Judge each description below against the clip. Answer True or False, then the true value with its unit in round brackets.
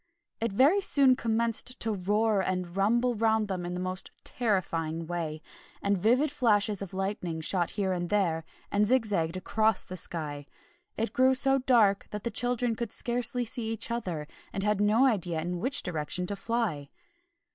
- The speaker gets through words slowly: False (175 wpm)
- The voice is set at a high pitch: True (205 Hz)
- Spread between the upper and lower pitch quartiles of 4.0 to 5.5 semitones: True (4.7 semitones)